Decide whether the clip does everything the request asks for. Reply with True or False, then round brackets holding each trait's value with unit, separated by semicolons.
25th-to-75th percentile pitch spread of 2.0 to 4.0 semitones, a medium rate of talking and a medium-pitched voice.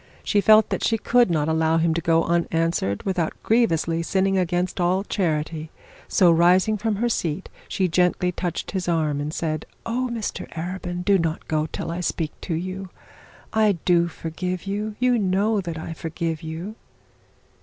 True (3.2 semitones; 170 wpm; 175 Hz)